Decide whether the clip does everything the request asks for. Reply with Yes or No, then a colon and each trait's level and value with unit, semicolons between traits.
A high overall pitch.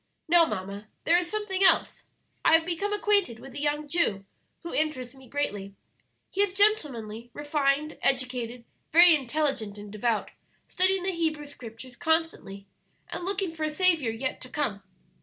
Yes: very high, 295 Hz